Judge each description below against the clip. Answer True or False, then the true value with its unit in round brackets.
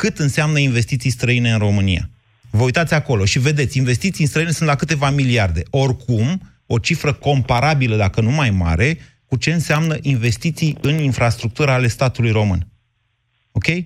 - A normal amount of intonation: True (4.4 semitones)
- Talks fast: False (155 wpm)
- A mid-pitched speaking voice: False (130 Hz)